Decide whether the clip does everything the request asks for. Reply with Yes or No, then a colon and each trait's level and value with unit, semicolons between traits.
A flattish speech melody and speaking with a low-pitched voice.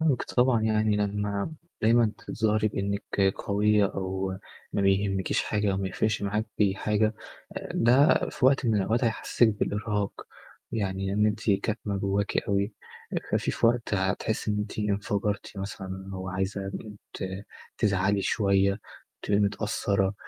Yes: narrow, 1.7 semitones; low, 105 Hz